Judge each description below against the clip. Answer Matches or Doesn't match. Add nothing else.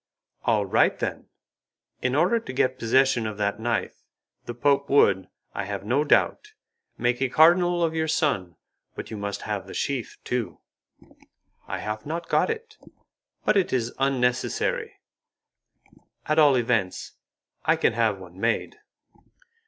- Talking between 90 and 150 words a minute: Matches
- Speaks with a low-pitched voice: Matches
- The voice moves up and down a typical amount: Doesn't match